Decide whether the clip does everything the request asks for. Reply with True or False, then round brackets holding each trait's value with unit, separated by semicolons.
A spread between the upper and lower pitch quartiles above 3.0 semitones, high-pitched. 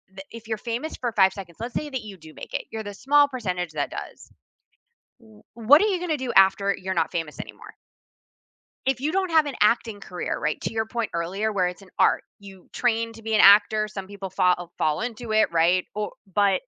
True (4.0 semitones; 215 Hz)